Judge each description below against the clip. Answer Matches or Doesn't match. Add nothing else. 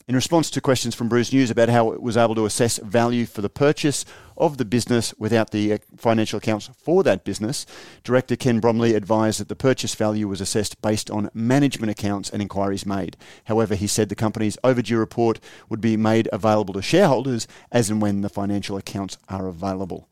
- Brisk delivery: Doesn't match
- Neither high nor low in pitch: Doesn't match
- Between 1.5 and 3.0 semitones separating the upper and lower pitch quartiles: Matches